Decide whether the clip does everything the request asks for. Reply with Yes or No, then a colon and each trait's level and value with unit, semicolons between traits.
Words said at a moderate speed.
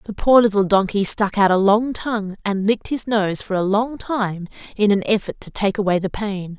No: fast, 230 wpm